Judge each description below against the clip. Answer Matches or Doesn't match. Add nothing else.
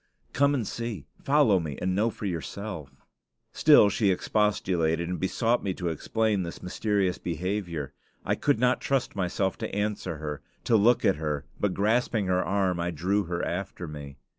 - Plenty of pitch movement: Doesn't match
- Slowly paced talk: Doesn't match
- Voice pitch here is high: Doesn't match